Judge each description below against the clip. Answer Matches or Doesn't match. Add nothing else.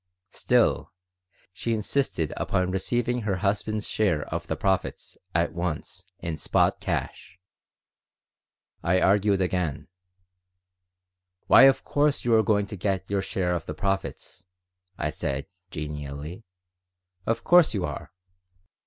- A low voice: Matches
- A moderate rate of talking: Doesn't match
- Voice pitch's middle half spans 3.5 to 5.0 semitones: Matches